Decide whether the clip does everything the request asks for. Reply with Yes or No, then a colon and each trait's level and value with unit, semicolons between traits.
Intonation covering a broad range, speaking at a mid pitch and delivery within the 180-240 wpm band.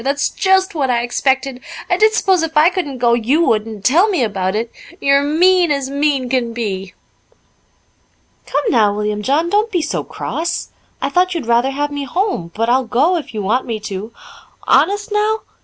No: wide, 6.8 semitones; very high, 275 Hz; average, 190 wpm